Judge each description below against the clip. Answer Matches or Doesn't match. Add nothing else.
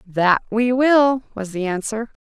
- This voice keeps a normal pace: Matches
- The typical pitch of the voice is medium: Doesn't match